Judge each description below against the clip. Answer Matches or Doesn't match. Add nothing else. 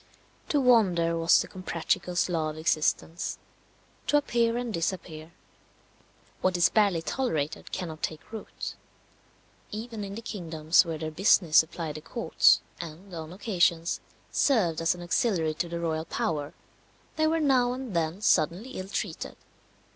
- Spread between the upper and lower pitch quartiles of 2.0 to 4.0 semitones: Doesn't match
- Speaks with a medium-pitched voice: Matches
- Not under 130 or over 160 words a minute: Matches